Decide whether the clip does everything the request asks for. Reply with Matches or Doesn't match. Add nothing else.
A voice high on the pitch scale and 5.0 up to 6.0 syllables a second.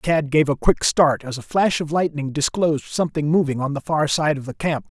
Doesn't match